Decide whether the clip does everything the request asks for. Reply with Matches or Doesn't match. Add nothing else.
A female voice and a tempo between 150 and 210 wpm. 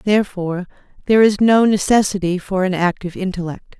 Doesn't match